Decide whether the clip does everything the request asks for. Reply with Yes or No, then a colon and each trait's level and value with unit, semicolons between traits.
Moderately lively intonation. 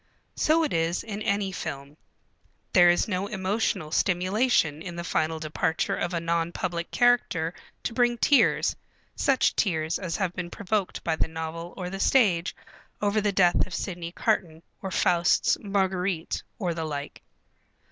Yes: average, 3.4 semitones